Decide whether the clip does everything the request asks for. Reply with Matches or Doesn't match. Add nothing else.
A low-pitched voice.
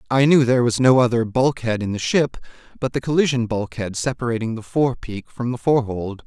Matches